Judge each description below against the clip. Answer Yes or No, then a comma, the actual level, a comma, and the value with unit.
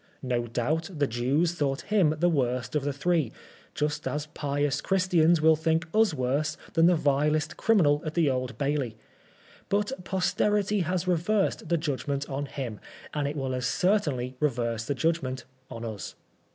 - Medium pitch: Yes, medium, 150 Hz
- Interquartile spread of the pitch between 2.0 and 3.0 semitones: No, average, 4.2 semitones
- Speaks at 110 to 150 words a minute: No, average, 165 wpm